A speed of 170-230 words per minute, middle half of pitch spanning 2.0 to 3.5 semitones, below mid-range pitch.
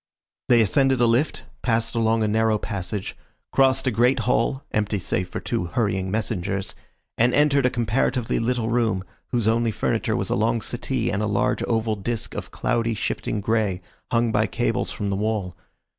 Yes: average, 175 wpm; narrow, 2.4 semitones; low, 115 Hz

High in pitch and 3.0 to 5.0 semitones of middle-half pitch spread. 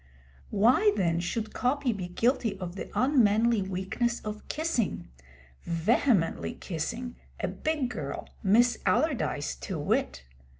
No: high, 220 Hz; wide, 5.4 semitones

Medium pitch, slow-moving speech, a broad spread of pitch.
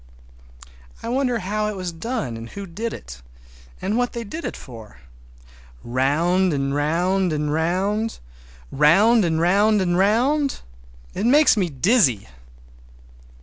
Yes: medium, 180 Hz; slow, 125 wpm; wide, 7.8 semitones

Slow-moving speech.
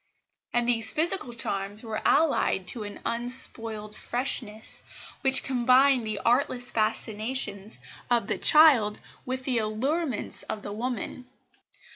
Yes: slow, 120 wpm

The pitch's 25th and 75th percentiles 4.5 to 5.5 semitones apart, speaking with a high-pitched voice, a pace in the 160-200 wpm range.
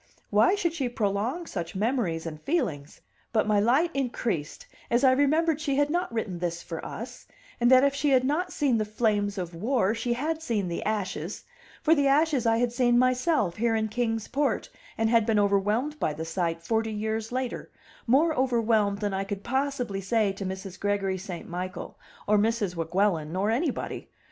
Yes: average, 5.1 semitones; high, 225 Hz; average, 190 wpm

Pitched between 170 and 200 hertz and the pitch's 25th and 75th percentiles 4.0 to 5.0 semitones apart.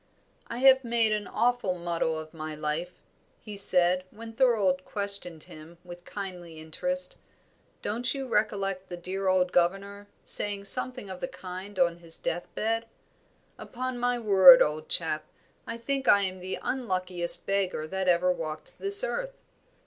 Yes: high, 190 Hz; average, 4.7 semitones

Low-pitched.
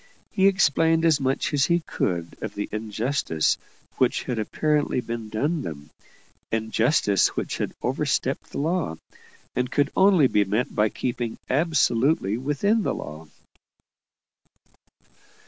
Yes: low, 125 Hz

